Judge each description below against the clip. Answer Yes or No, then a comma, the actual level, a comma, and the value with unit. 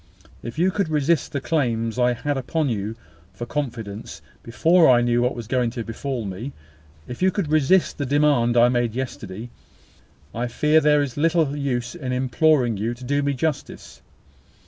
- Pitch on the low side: Yes, low, 130 Hz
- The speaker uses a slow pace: No, average, 175 wpm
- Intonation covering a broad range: No, average, 3.8 semitones